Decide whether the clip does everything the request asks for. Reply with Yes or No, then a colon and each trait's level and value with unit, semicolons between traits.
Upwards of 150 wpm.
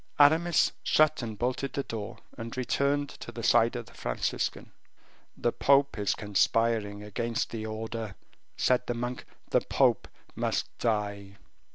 No: average, 145 wpm